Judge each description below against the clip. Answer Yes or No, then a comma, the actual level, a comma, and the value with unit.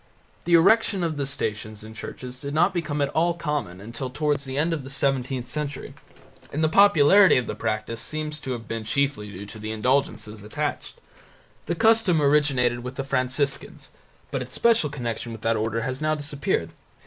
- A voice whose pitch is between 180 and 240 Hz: No, medium, 140 Hz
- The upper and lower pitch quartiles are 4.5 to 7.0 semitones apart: Yes, average, 4.8 semitones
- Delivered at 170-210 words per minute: Yes, average, 185 wpm